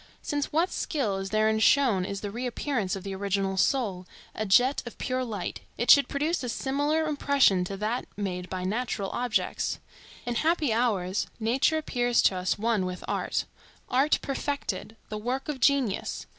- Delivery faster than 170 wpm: No, average, 165 wpm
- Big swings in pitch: Yes, wide, 5.7 semitones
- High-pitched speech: Yes, high, 235 Hz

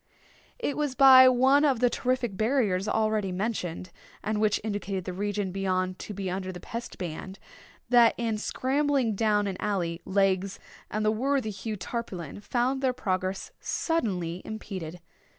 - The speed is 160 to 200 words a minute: No, average, 150 wpm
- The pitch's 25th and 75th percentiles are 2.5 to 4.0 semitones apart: No, average, 4.6 semitones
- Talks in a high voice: Yes, high, 210 Hz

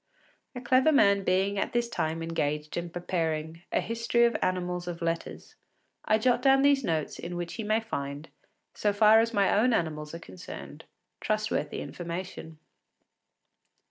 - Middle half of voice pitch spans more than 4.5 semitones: Yes, wide, 5.4 semitones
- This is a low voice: No, medium, 185 Hz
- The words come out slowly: No, average, 155 wpm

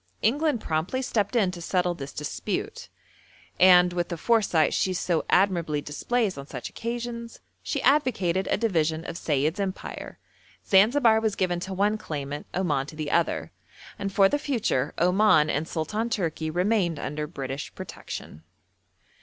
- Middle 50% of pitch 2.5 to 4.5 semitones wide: No, wide, 5.5 semitones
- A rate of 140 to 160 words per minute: Yes, average, 150 wpm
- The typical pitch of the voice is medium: Yes, medium, 180 Hz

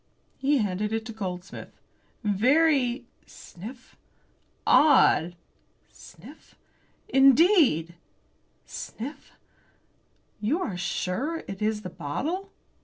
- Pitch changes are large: Yes, wide, 6.9 semitones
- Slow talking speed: Yes, slow, 85 wpm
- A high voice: Yes, high, 225 Hz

